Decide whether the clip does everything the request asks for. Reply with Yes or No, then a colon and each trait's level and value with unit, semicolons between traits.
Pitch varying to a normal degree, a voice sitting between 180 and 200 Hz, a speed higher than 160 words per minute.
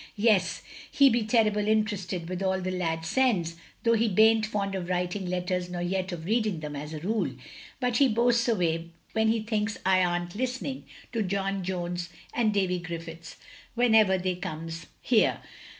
Yes: average, 3.9 semitones; high, 190 Hz; average, 190 wpm